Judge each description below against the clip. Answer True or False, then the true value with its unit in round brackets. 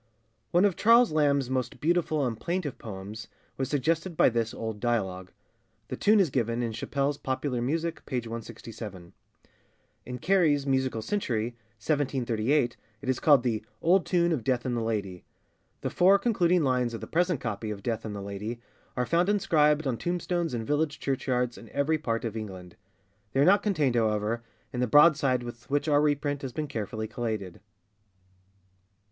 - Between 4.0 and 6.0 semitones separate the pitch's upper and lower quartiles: True (5.3 semitones)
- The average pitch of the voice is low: True (130 Hz)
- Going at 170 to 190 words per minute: True (175 wpm)